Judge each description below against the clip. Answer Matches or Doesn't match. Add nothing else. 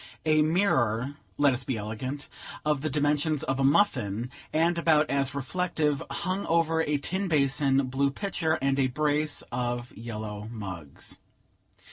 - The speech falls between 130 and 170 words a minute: Matches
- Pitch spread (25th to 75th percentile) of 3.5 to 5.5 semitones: Matches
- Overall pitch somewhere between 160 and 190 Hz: Doesn't match